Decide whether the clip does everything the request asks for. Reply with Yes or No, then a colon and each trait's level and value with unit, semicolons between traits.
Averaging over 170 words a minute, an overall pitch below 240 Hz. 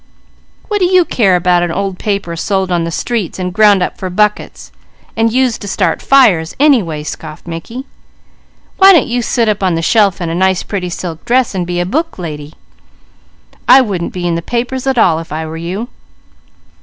Yes: average, 200 wpm; high, 190 Hz